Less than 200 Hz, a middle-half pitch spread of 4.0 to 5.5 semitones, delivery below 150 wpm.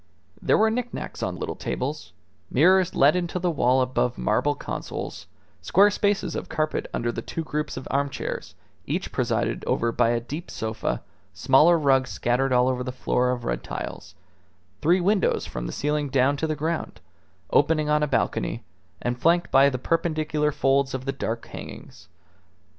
No: medium, 140 Hz; average, 4.5 semitones; average, 170 wpm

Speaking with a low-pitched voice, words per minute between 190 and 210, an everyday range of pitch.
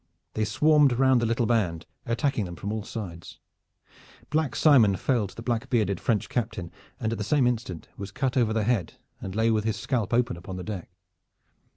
Yes: low, 110 Hz; average, 195 wpm; average, 3.6 semitones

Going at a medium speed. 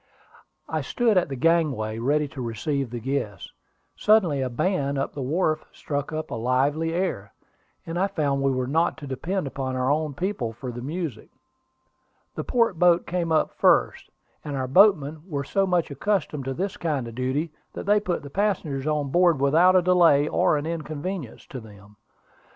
Yes: average, 180 wpm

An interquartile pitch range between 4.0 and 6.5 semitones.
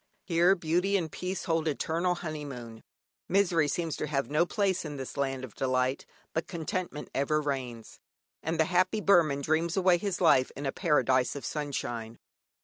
Yes: average, 4.3 semitones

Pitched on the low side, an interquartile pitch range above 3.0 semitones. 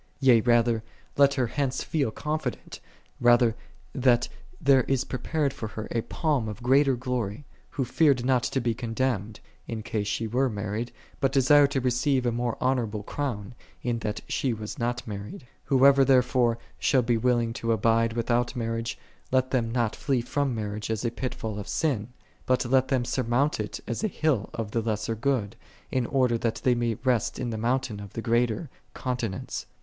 No: low, 120 Hz; narrow, 2.6 semitones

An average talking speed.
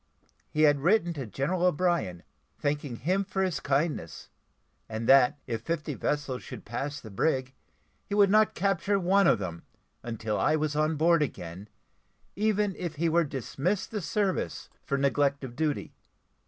Yes: average, 160 wpm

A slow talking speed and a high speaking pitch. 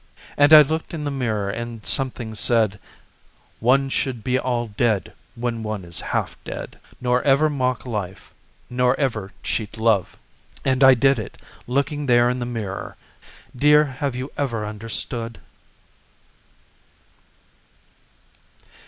No: slow, 130 wpm; low, 125 Hz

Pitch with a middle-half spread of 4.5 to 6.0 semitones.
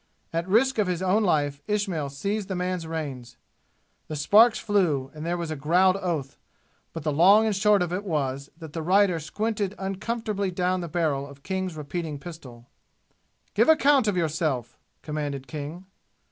Yes: average, 4.8 semitones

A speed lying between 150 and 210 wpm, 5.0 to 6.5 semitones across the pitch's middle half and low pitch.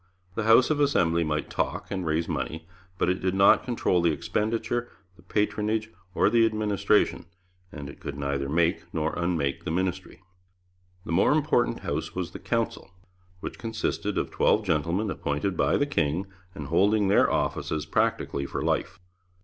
Yes: average, 165 wpm; average, 5.3 semitones; very low, 90 Hz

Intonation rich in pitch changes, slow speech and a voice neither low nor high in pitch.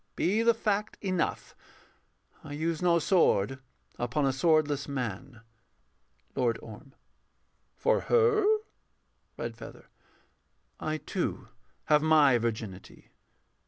Yes: wide, 6.2 semitones; slow, 95 wpm; medium, 150 Hz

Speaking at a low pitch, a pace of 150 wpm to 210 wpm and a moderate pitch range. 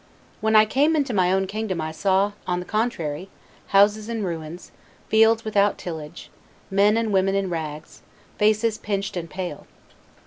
No: high, 195 Hz; average, 160 wpm; average, 3.4 semitones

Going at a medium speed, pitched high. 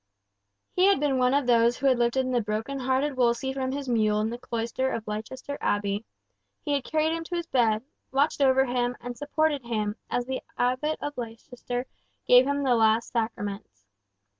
Yes: average, 190 wpm; very high, 250 Hz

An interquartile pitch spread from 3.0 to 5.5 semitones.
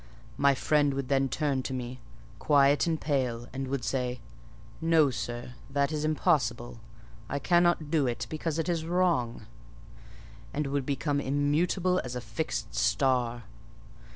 Yes: average, 3.6 semitones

